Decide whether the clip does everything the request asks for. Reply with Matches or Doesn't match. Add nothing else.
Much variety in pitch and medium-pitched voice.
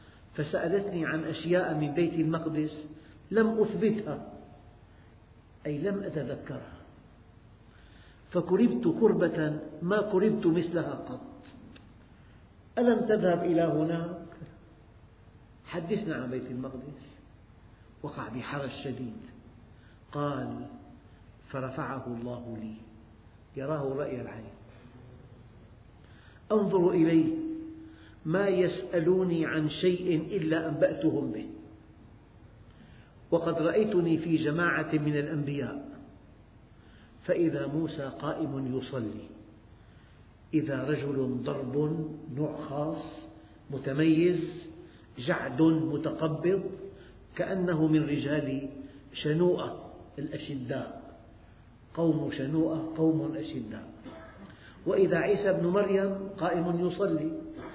Matches